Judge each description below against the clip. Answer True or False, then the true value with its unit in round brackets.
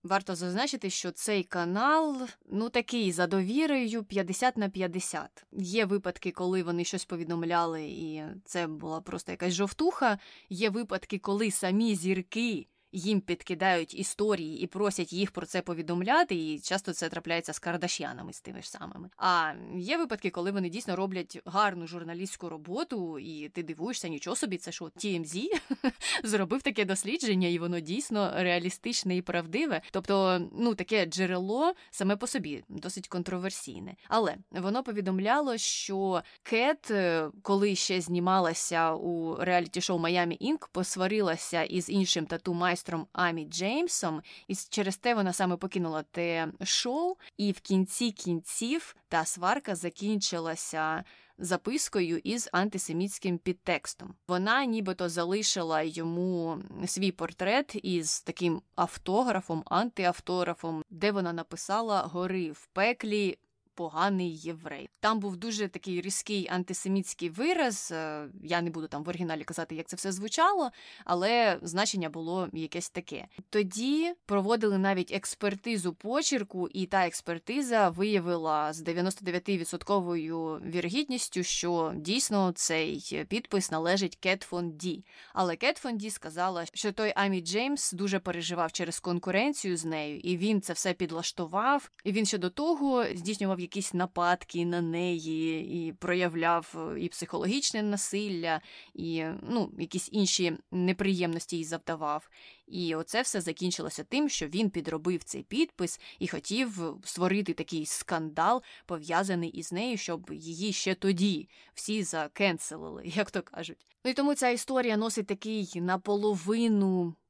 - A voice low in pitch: False (185 Hz)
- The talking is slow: False (130 wpm)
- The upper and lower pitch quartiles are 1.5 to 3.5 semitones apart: True (3.1 semitones)